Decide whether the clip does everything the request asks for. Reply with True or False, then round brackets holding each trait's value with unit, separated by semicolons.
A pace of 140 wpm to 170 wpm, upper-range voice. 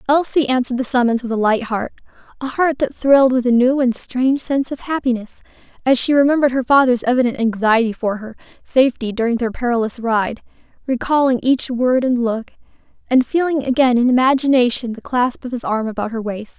False (185 wpm; 250 Hz)